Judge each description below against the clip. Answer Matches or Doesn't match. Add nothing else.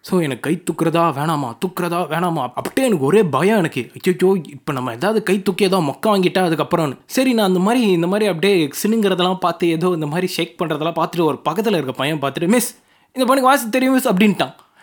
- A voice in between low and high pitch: Matches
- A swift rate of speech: Matches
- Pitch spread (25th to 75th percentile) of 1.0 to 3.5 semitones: Doesn't match